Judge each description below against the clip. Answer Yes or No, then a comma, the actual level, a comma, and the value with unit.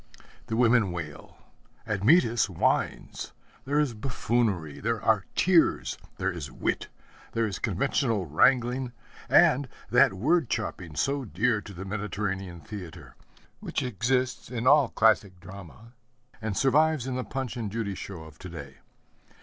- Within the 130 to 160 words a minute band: Yes, average, 140 wpm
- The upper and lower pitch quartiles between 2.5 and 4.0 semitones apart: No, average, 4.9 semitones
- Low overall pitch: Yes, low, 110 Hz